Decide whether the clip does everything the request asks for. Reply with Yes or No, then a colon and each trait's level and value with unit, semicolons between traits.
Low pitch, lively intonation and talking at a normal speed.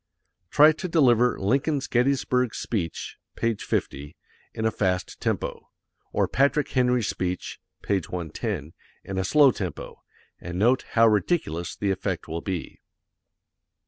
No: low, 110 Hz; wide, 5.9 semitones; slow, 130 wpm